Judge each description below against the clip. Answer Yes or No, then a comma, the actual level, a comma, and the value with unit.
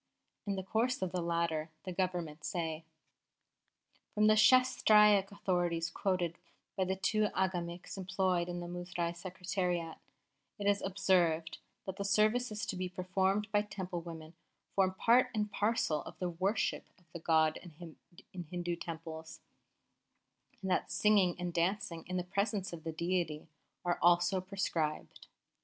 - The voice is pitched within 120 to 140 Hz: No, medium, 180 Hz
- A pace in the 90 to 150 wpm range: Yes, average, 145 wpm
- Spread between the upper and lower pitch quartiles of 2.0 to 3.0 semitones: Yes, narrow, 2.6 semitones